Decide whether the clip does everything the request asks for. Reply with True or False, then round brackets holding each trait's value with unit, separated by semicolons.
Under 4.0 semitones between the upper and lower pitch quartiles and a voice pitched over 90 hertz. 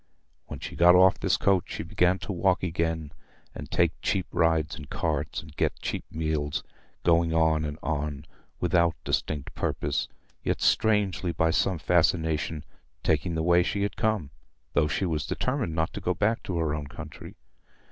False (2.7 semitones; 80 Hz)